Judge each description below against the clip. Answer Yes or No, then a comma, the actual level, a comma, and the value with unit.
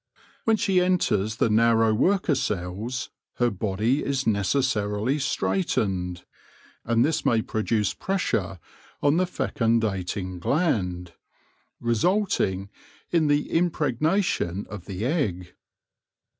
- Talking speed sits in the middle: No, slow, 100 wpm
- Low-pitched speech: Yes, low, 115 Hz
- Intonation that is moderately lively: No, wide, 7.1 semitones